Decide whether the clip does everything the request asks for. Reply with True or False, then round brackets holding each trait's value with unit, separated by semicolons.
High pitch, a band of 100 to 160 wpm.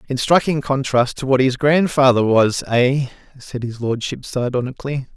False (130 Hz; 150 wpm)